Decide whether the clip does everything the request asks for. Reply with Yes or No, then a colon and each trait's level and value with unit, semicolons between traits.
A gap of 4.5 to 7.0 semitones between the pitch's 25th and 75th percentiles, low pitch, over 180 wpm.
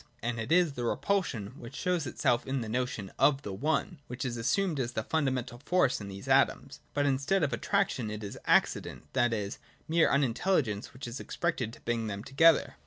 Yes: average, 5.2 semitones; low, 130 Hz; average, 195 wpm